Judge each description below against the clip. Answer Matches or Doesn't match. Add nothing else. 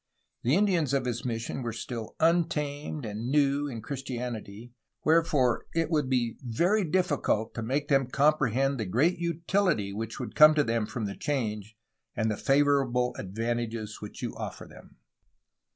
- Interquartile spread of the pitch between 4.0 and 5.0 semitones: Matches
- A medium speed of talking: Matches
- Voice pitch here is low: Matches